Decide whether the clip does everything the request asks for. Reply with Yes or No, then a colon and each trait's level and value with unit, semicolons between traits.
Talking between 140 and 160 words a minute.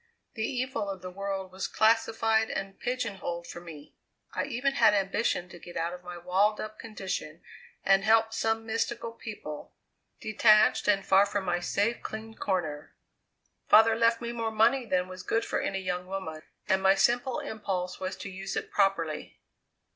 No: average, 175 wpm